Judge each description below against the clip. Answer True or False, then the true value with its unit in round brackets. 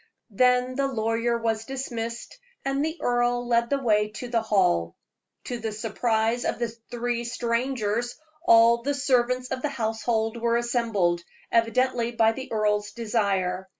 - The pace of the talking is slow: False (150 wpm)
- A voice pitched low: False (235 Hz)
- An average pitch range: False (2.0 semitones)